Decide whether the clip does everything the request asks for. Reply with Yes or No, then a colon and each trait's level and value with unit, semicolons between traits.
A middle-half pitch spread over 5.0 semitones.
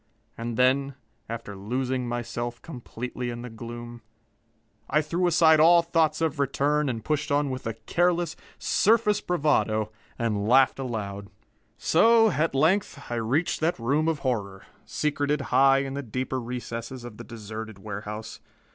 No: average, 4.7 semitones